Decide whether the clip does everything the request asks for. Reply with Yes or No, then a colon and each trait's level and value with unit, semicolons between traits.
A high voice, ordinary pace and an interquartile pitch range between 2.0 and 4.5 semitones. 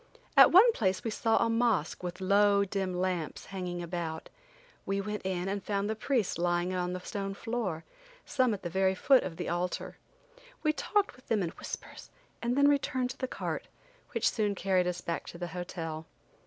Yes: high, 195 Hz; average, 195 wpm; average, 4.1 semitones